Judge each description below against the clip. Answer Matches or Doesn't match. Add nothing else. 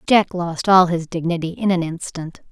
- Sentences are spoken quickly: Doesn't match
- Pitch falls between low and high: Matches